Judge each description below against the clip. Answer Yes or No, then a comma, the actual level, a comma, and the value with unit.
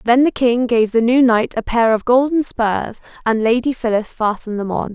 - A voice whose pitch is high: Yes, high, 235 Hz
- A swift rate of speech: Yes, fast, 220 wpm